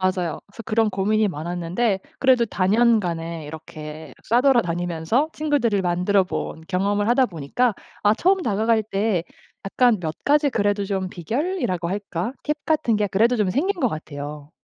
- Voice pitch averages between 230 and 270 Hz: No, high, 205 Hz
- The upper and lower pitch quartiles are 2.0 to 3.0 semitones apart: No, average, 5.3 semitones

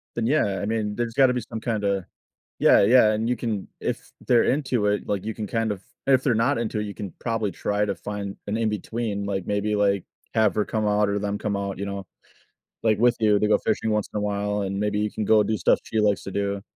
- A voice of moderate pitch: No, low, 105 Hz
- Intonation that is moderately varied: No, narrow, 1.8 semitones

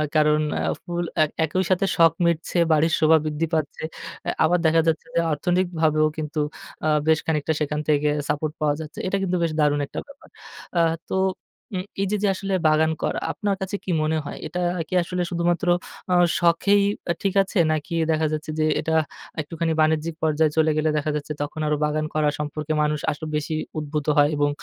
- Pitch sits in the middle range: Yes, medium, 155 Hz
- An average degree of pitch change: No, narrow, 2.1 semitones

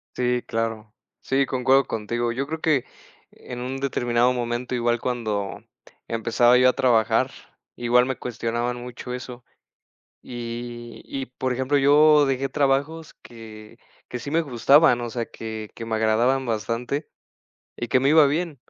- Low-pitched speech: Yes, low, 125 Hz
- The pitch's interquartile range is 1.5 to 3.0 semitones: Yes, narrow, 2.4 semitones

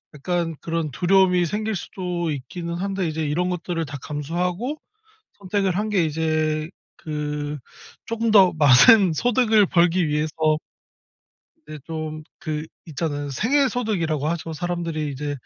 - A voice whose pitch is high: No, medium, 170 Hz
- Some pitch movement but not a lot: Yes, average, 3.6 semitones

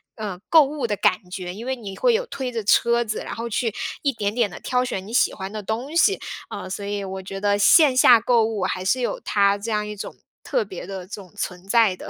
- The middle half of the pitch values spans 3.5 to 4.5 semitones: Yes, average, 3.9 semitones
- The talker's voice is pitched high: Yes, high, 215 Hz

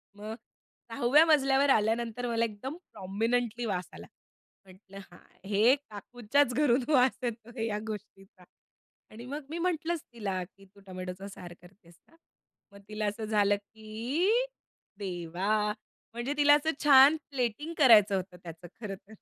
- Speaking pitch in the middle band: No, high, 220 Hz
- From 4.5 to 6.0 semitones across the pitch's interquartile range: Yes, average, 4.8 semitones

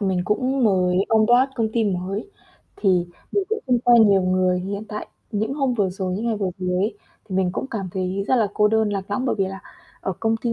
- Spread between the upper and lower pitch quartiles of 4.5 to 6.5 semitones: No, average, 3.6 semitones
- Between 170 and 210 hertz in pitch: Yes, high, 205 Hz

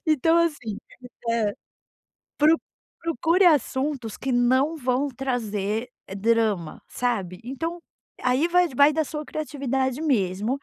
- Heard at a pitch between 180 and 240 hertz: No, very high, 260 Hz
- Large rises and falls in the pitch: No, average, 4.9 semitones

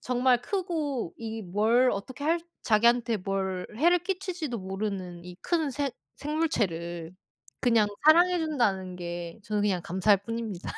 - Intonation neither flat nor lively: No, wide, 7.5 semitones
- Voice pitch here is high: Yes, high, 225 Hz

